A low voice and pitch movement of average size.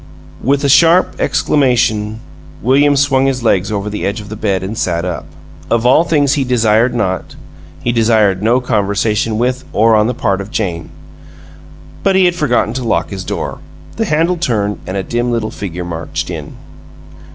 Yes: low, 115 Hz; average, 4.6 semitones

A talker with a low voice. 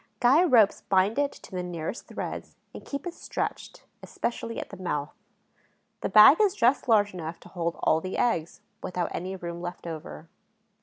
No: high, 190 Hz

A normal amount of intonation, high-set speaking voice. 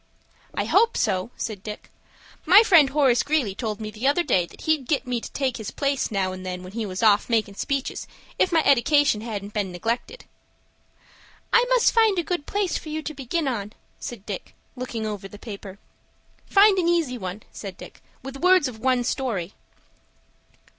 No: wide, 6.9 semitones; high, 245 Hz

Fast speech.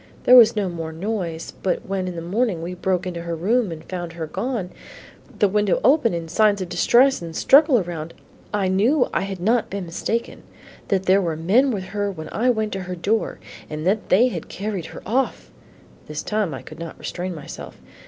Yes: fast, 210 wpm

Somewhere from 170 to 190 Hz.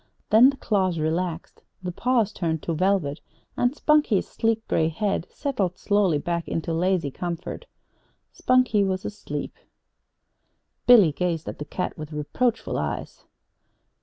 Yes: medium, 185 Hz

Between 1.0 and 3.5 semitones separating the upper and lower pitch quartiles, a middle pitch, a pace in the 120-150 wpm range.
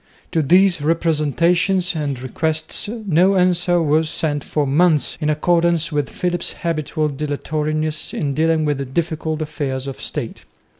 Yes: narrow, 2.5 semitones; medium, 155 Hz; slow, 135 wpm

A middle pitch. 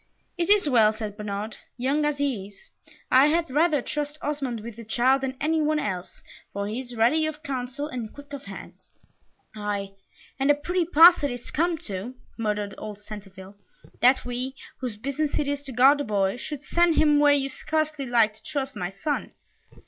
No: very high, 265 Hz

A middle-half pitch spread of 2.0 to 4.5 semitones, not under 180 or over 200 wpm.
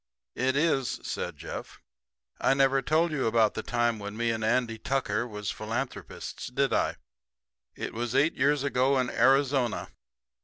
No: average, 3.2 semitones; average, 155 wpm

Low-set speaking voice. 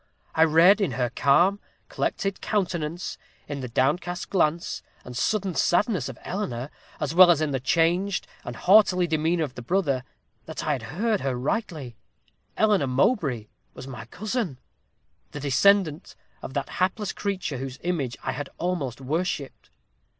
No: medium, 160 Hz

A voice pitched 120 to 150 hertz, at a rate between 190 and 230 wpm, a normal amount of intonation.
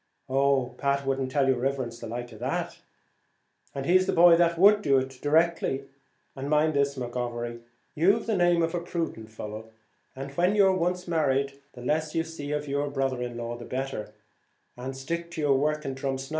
Yes: medium, 140 Hz; average, 195 wpm; average, 4.1 semitones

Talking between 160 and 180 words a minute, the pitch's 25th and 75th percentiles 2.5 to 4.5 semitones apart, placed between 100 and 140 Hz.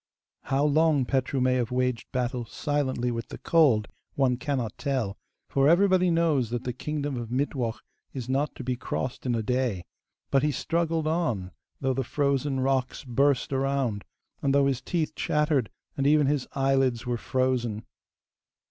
Yes: average, 165 wpm; average, 2.8 semitones; low, 135 Hz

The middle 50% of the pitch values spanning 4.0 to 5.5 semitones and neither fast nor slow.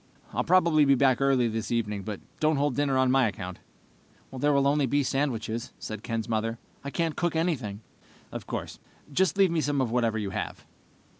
Yes: average, 4.5 semitones; average, 195 wpm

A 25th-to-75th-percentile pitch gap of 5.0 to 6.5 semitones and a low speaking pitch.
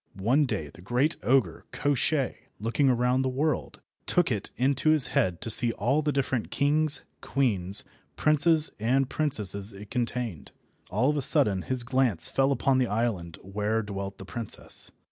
Yes: average, 5.3 semitones; low, 125 Hz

